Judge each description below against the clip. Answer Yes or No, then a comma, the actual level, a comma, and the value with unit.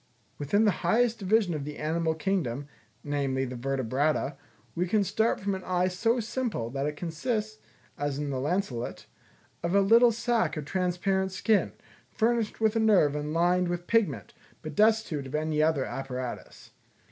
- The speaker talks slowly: No, average, 165 wpm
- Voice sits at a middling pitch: Yes, medium, 175 Hz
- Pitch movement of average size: No, wide, 6.7 semitones